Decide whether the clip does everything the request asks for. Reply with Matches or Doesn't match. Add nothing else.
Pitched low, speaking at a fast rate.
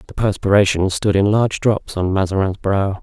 Doesn't match